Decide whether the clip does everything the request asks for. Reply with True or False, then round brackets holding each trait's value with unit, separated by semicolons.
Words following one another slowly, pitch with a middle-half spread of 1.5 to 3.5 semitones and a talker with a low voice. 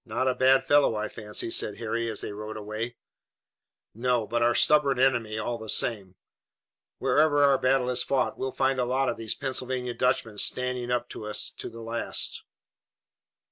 False (180 wpm; 2.8 semitones; 120 Hz)